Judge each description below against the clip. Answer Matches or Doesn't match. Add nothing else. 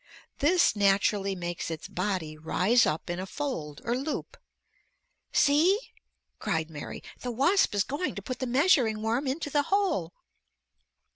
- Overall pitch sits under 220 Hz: Doesn't match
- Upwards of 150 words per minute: Doesn't match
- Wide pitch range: Matches